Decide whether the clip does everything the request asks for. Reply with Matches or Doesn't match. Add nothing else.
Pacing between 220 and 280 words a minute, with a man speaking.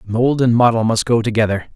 Doesn't match